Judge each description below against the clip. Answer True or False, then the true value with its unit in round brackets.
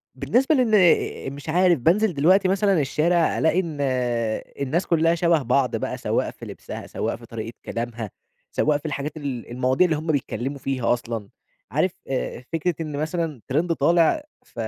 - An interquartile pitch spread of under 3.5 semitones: False (4.8 semitones)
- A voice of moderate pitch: True (155 Hz)